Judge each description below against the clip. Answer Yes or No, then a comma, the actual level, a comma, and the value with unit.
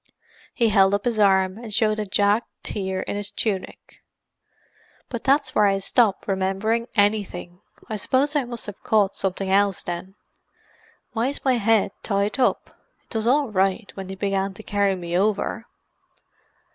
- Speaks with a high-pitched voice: Yes, high, 205 Hz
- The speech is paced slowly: No, average, 165 wpm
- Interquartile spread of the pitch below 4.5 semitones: Yes, average, 2.8 semitones